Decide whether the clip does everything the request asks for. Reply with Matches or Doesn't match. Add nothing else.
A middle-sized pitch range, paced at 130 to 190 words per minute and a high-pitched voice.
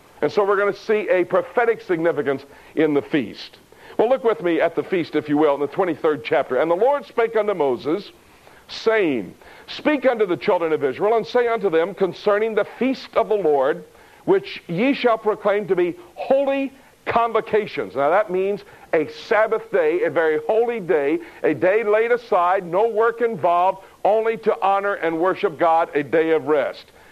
Matches